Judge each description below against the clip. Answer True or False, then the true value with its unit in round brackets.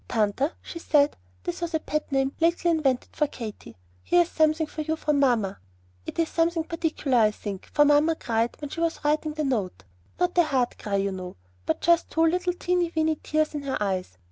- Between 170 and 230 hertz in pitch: False (300 Hz)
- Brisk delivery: True (210 wpm)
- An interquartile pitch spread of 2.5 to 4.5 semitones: False (5.4 semitones)